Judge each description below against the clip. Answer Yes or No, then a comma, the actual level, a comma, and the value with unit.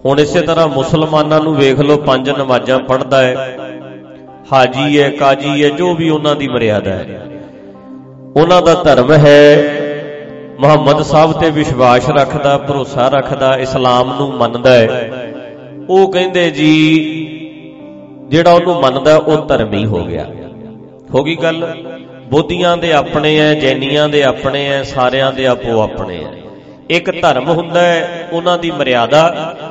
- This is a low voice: No, medium, 145 Hz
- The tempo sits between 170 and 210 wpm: No, average, 140 wpm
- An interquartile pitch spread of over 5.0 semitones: No, average, 3.1 semitones